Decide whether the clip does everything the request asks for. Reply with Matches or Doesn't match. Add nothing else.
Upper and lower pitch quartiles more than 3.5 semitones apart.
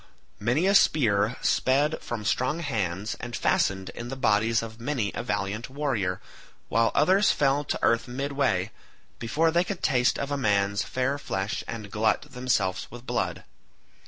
Matches